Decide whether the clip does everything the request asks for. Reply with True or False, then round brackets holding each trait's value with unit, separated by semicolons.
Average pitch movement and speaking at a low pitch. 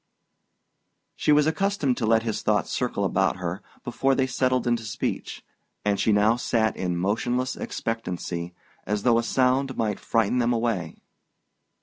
True (3.7 semitones; 115 Hz)